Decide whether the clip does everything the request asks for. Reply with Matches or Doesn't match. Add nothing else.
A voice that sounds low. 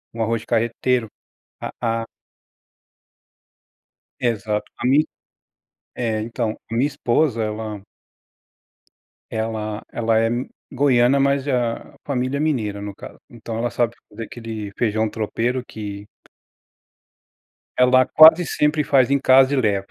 Matches